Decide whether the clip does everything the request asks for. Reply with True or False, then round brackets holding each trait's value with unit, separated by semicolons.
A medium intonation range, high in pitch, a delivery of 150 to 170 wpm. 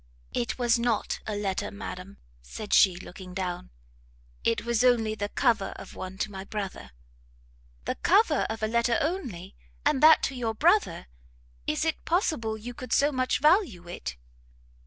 True (4.8 semitones; 225 Hz; 160 wpm)